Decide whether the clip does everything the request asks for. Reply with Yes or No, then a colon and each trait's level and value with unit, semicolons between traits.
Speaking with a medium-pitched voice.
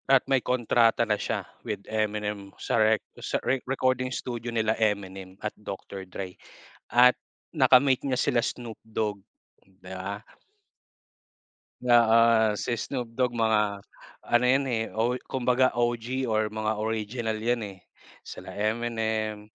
No: low, 115 Hz